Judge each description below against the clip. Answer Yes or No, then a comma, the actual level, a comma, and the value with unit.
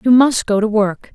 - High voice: Yes, high, 220 Hz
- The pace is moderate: No, fast, 265 wpm